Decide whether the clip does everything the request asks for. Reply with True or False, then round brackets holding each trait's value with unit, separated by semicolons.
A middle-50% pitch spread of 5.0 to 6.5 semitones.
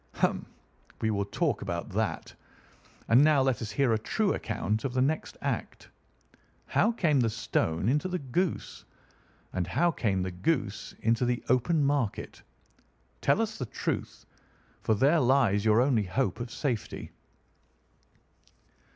True (5.3 semitones)